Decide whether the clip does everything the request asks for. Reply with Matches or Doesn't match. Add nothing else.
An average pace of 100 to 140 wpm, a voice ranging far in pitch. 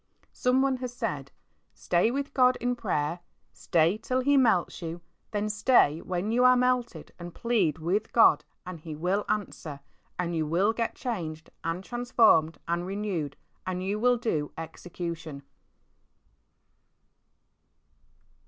Matches